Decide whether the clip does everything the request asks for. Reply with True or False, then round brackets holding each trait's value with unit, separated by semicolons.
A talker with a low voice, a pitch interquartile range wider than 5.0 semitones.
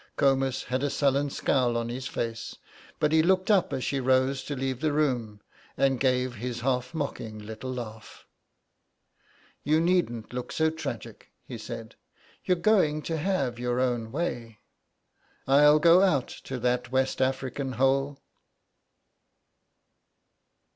False (130 Hz; 3.3 semitones)